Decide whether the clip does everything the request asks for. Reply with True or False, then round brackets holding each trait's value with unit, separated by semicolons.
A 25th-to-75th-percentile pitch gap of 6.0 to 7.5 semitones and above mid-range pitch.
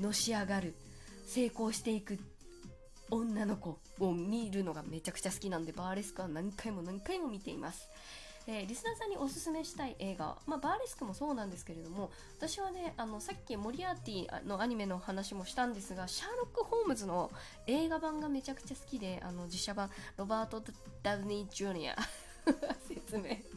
True (6.3 semitones; 210 Hz)